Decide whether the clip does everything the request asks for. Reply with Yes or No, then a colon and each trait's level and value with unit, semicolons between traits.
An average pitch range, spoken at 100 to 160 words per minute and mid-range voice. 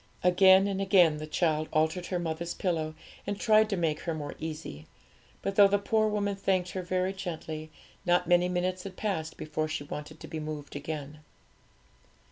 No: average, 3.5 semitones; average, 180 wpm; medium, 175 Hz